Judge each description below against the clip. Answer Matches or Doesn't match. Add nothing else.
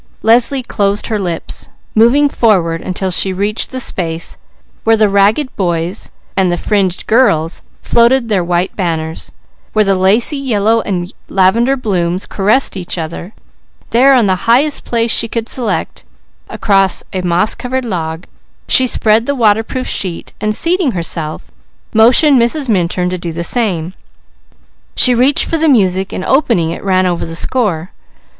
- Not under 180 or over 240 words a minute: Doesn't match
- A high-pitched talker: Matches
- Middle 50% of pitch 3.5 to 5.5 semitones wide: Matches